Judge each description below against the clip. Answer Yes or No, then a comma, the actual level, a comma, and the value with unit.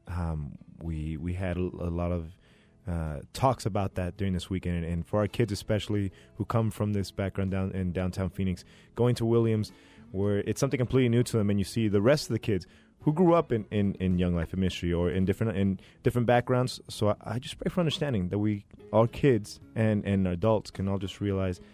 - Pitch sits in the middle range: No, low, 100 Hz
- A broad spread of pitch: No, average, 3.7 semitones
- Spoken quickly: Yes, fast, 230 wpm